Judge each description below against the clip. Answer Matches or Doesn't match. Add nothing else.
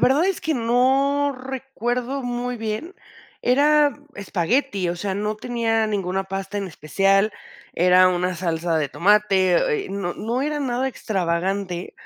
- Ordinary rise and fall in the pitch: Doesn't match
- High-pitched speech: Matches